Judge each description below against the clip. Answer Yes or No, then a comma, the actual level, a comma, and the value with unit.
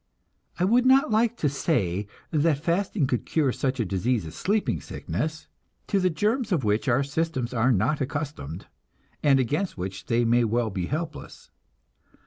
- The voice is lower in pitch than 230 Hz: Yes, medium, 140 Hz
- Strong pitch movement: Yes, wide, 6.5 semitones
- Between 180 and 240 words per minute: No, average, 165 wpm